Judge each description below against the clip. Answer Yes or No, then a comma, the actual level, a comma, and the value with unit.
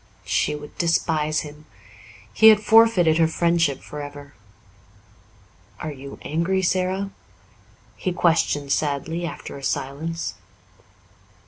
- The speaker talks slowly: Yes, slow, 110 wpm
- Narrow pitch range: No, average, 3.3 semitones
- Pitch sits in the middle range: Yes, medium, 160 Hz